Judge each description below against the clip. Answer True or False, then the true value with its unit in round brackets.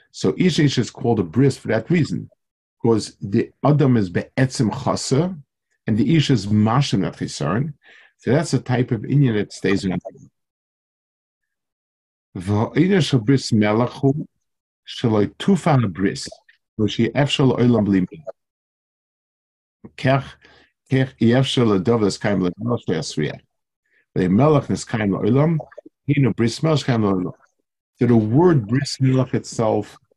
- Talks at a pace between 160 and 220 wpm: False (140 wpm)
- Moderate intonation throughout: True (4.7 semitones)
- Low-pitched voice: True (125 Hz)